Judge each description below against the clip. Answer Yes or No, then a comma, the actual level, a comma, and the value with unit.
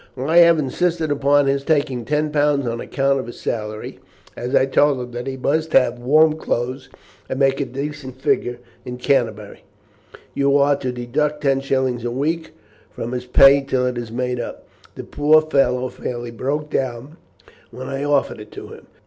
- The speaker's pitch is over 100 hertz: Yes, low, 135 Hz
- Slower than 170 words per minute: No, average, 185 wpm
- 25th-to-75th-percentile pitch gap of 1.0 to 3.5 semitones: Yes, average, 2.9 semitones